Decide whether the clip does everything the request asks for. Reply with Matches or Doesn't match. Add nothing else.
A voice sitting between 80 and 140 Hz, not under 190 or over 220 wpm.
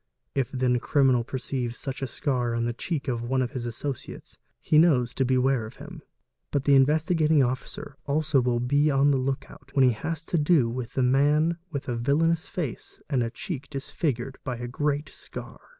Matches